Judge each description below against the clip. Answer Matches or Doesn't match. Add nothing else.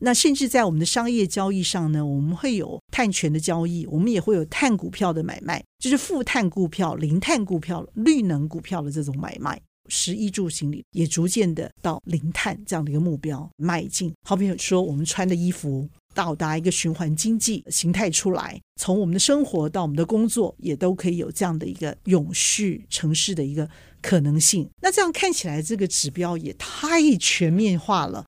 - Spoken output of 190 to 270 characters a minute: Doesn't match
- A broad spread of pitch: Doesn't match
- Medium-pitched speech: Matches